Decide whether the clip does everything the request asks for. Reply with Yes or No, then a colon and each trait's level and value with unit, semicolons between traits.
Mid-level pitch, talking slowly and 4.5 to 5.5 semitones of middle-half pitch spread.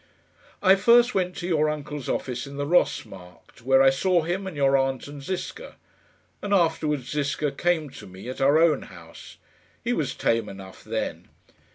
No: medium, 145 Hz; average, 180 wpm; average, 4.8 semitones